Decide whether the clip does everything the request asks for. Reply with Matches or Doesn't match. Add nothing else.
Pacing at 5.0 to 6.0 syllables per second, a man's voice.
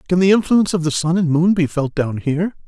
Doesn't match